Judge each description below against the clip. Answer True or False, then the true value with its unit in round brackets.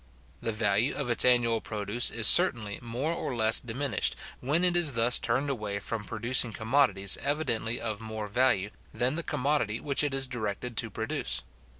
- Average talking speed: True (175 wpm)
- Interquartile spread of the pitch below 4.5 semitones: True (3.9 semitones)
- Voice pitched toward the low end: True (120 Hz)